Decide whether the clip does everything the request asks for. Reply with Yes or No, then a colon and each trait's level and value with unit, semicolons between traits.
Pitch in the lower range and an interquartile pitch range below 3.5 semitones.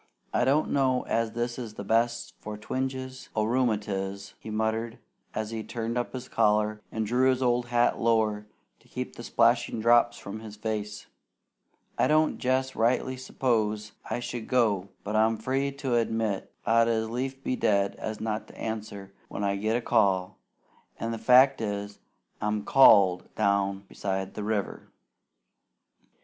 Yes: low, 110 Hz; average, 2.7 semitones